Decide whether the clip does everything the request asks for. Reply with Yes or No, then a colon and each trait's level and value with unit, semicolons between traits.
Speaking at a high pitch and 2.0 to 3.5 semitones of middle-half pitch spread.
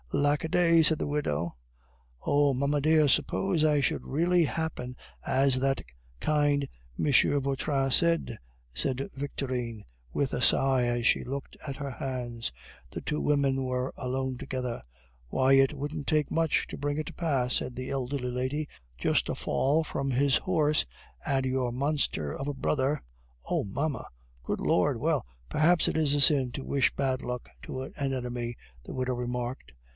No: low, 135 Hz; narrow, 2.6 semitones